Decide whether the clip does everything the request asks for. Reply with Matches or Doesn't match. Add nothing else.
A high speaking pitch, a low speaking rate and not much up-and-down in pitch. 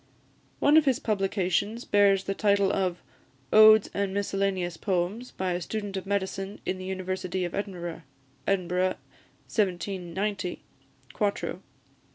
Matches